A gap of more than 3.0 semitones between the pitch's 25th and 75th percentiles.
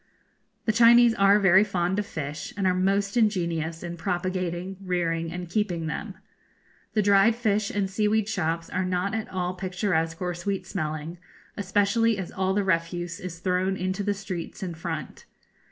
No: average, 2.7 semitones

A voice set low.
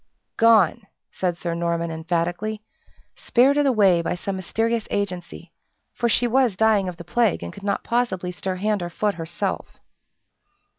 No: high, 195 Hz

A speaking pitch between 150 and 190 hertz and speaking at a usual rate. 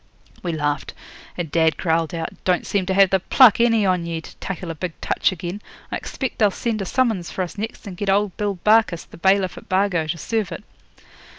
No: medium, 185 Hz; fast, 220 wpm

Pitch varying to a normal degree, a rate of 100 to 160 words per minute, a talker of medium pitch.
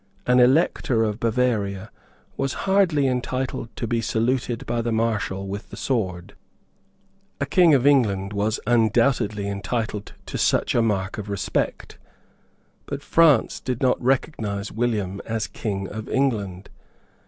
No: average, 4.0 semitones; slow, 135 wpm; low, 115 Hz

